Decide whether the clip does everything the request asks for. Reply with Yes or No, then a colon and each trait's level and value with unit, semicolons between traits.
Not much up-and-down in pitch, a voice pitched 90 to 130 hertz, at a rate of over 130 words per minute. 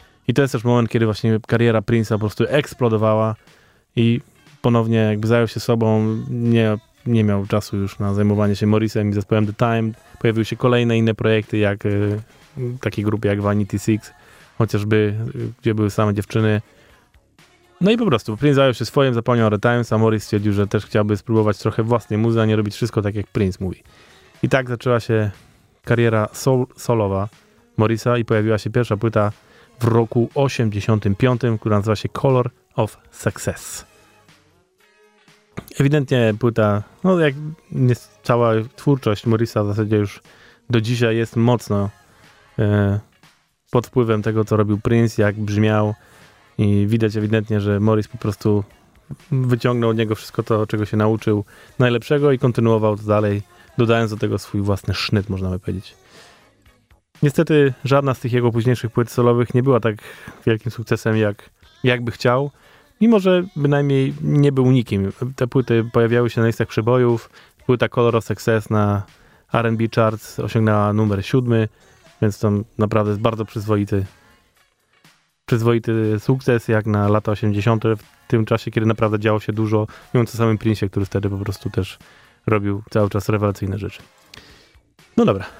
Yes: narrow, 2.3 semitones; low, 110 Hz; fast, 160 wpm